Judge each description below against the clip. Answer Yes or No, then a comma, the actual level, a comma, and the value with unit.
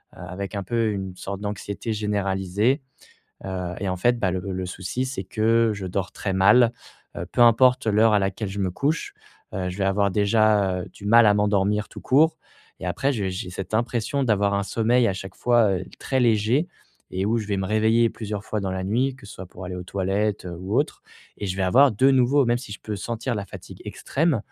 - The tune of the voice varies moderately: Yes, average, 3.4 semitones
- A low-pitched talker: Yes, low, 105 Hz